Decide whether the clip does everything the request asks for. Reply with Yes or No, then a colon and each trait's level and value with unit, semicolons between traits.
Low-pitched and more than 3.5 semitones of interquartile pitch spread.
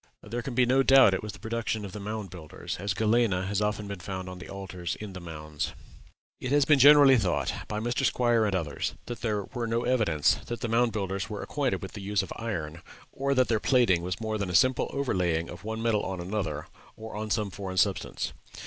Yes: low, 105 Hz; average, 4.0 semitones